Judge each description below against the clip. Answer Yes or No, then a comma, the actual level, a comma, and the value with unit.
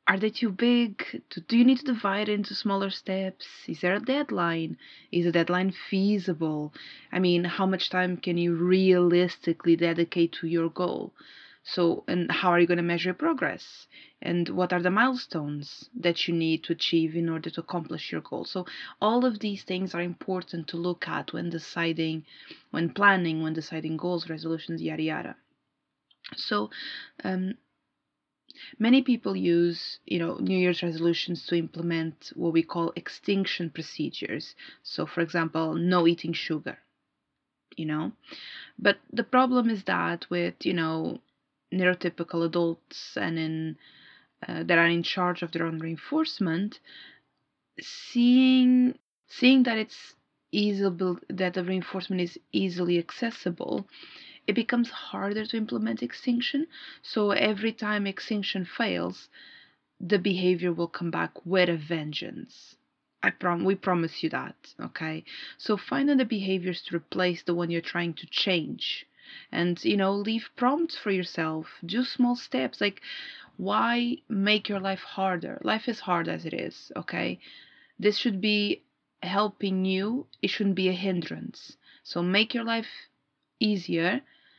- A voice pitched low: No, medium, 185 Hz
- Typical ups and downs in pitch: Yes, average, 4.2 semitones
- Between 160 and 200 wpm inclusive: No, average, 150 wpm